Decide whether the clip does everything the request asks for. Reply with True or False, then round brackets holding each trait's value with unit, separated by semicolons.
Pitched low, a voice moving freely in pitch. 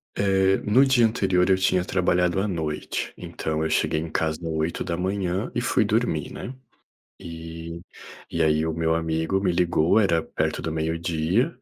False (85 Hz; 2.9 semitones)